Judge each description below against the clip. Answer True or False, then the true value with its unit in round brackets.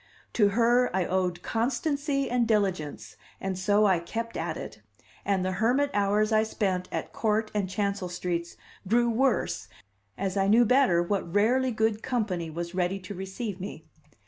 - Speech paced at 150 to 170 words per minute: True (165 wpm)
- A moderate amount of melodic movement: True (3.7 semitones)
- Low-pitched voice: False (205 Hz)